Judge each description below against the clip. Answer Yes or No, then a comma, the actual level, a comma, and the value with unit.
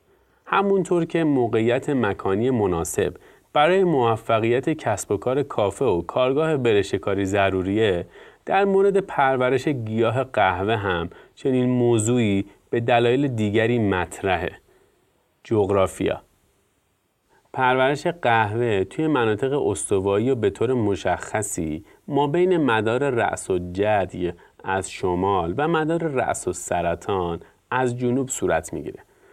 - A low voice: Yes, low, 125 Hz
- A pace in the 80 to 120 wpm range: Yes, average, 110 wpm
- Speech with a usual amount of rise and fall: No, wide, 7.0 semitones